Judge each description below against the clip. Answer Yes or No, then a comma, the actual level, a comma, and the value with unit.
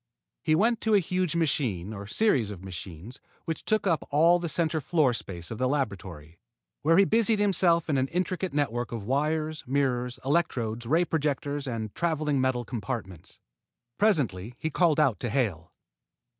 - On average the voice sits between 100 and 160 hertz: Yes, medium, 140 Hz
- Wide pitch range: Yes, wide, 6.6 semitones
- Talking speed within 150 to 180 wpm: Yes, average, 165 wpm